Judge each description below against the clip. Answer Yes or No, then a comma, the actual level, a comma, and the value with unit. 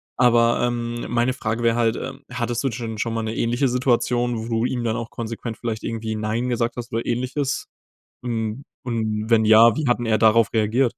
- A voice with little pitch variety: Yes, narrow, 1.5 semitones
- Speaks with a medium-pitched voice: No, low, 115 Hz